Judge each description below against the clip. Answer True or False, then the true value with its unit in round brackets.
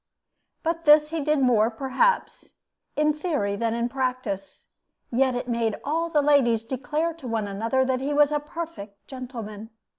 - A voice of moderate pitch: False (260 Hz)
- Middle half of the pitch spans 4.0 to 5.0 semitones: True (4.7 semitones)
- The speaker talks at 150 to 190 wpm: True (160 wpm)